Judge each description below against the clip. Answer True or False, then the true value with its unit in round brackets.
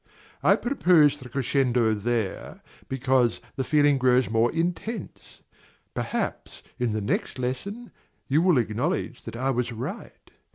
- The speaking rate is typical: False (130 wpm)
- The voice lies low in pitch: True (130 Hz)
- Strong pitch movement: False (4.4 semitones)